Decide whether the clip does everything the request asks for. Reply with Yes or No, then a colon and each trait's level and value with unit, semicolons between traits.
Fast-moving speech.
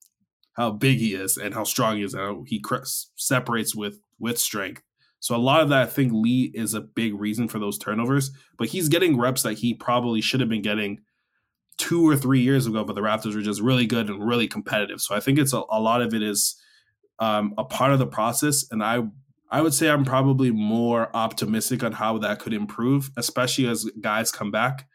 Yes: fast, 225 wpm